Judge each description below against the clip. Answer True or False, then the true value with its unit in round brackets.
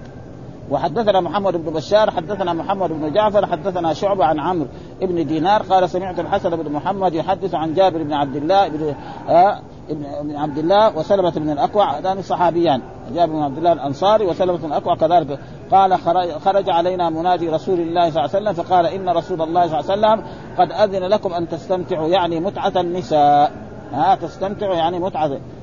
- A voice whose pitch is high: False (175 Hz)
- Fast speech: True (170 wpm)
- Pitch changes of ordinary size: True (3.6 semitones)